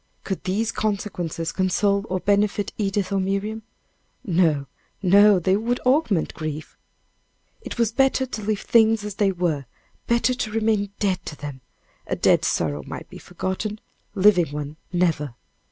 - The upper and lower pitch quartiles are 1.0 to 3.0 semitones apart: No, average, 3.8 semitones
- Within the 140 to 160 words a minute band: Yes, average, 150 wpm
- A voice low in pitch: No, high, 195 Hz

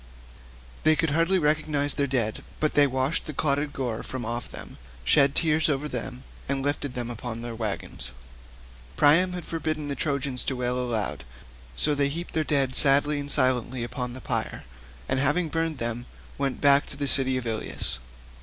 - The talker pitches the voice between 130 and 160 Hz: Yes, medium, 140 Hz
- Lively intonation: No, average, 3.3 semitones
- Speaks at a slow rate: No, average, 180 wpm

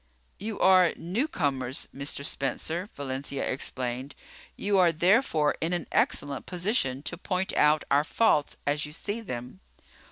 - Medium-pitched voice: Yes, medium, 155 Hz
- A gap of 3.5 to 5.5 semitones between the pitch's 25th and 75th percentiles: Yes, average, 5.0 semitones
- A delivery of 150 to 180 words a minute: No, slow, 135 wpm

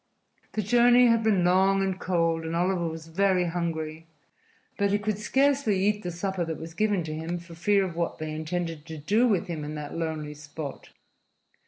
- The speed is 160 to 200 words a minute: Yes, average, 190 wpm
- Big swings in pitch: No, average, 3.8 semitones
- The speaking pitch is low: No, medium, 175 Hz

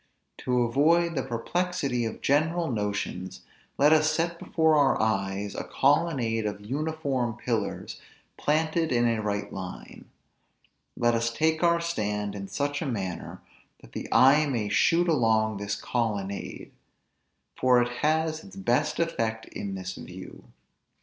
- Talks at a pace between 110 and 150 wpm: Yes, average, 140 wpm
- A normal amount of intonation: No, wide, 6.8 semitones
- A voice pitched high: No, low, 125 Hz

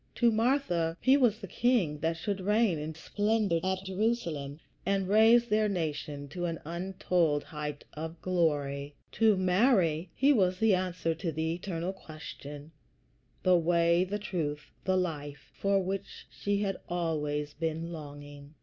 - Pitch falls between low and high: Yes, medium, 175 Hz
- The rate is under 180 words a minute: Yes, average, 150 wpm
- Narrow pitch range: No, average, 4.3 semitones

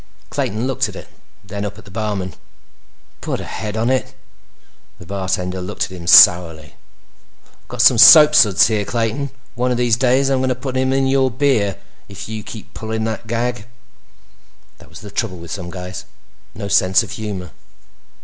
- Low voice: Yes, low, 110 Hz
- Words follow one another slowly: No, average, 180 wpm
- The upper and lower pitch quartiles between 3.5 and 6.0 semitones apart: Yes, average, 4.7 semitones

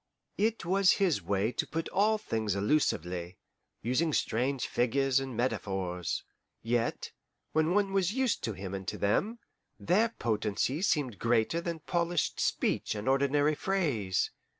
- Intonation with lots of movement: Yes, wide, 8.4 semitones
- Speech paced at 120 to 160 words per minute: Yes, average, 140 wpm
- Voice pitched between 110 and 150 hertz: Yes, low, 135 Hz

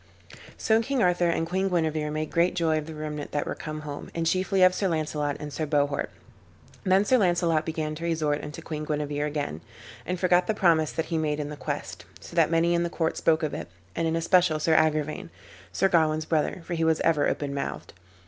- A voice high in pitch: No, medium, 160 Hz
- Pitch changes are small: Yes, narrow, 2.3 semitones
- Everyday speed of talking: No, fast, 220 wpm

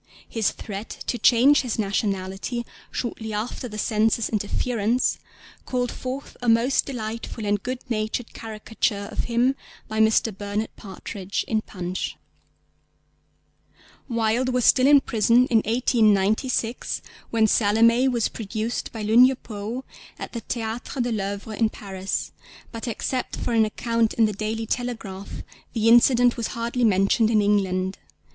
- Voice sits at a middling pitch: No, high, 225 Hz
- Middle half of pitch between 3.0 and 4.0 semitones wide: No, narrow, 2.5 semitones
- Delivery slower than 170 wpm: Yes, average, 140 wpm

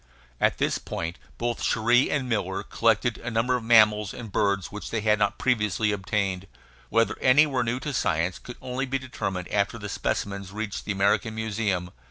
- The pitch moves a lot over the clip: No, average, 3.4 semitones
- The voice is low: Yes, low, 110 Hz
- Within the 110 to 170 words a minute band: No, average, 185 wpm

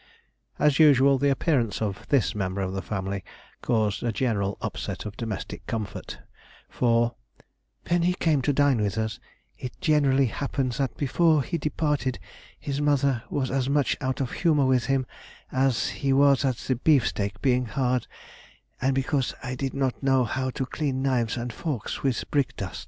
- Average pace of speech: Yes, average, 170 wpm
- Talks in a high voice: No, low, 130 Hz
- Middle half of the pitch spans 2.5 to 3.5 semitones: Yes, average, 3.2 semitones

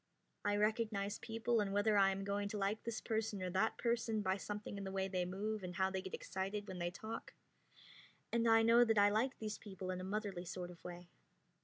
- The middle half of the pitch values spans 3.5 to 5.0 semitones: No, narrow, 2.4 semitones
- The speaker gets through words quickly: Yes, fast, 225 wpm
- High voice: Yes, high, 205 Hz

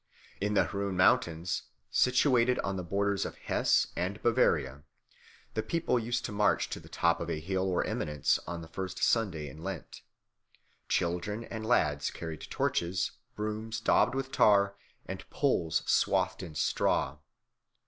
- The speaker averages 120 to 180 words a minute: Yes, average, 150 wpm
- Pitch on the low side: Yes, very low, 95 Hz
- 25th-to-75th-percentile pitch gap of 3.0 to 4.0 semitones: No, average, 4.5 semitones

